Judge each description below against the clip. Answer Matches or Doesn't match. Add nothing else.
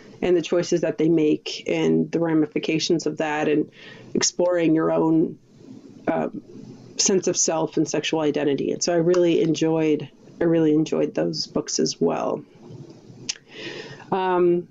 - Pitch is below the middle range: Doesn't match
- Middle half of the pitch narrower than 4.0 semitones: Matches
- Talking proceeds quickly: Doesn't match